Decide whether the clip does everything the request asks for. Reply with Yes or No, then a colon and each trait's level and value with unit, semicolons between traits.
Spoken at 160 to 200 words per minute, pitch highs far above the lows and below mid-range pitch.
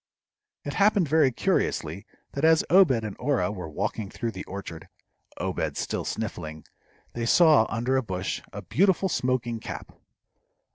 No: average, 145 wpm; wide, 8.1 semitones; low, 120 Hz